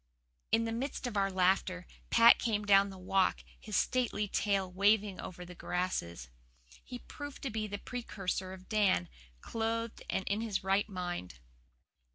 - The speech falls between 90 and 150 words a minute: No, average, 165 wpm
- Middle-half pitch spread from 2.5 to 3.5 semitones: Yes, average, 3.2 semitones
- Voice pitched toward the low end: No, high, 200 Hz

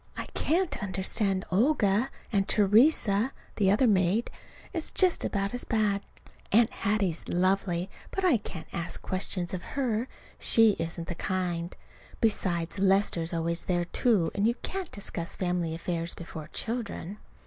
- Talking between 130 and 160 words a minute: Yes, average, 140 wpm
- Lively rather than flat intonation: No, average, 4.3 semitones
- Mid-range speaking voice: No, high, 195 Hz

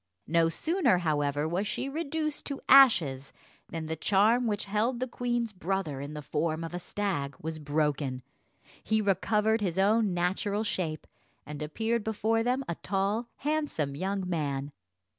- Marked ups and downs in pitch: Yes, wide, 6.4 semitones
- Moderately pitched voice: No, high, 195 Hz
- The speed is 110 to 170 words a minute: Yes, average, 155 wpm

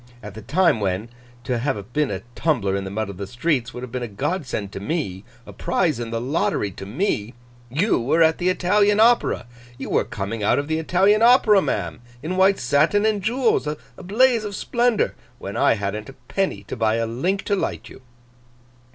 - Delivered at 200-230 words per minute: Yes, fast, 205 wpm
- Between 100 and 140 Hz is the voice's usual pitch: Yes, low, 135 Hz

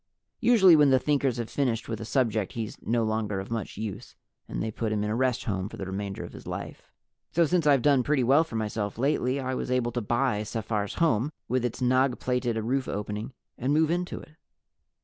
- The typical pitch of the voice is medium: No, low, 120 Hz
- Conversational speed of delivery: No, fast, 220 wpm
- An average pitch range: Yes, average, 4.0 semitones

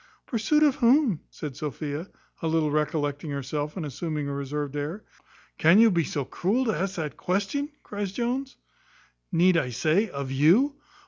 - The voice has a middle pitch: Yes, medium, 165 Hz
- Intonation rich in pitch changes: Yes, wide, 6.5 semitones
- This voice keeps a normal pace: Yes, average, 165 wpm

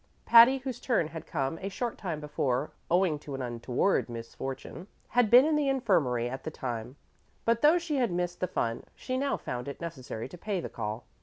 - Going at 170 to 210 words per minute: Yes, fast, 205 wpm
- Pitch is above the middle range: No, medium, 170 Hz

